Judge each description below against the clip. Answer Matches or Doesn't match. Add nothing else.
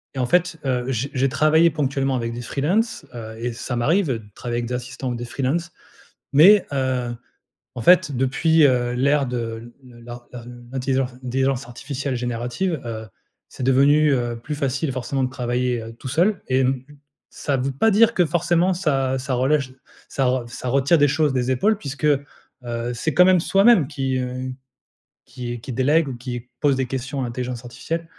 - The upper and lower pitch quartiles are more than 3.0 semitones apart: Matches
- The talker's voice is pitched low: Matches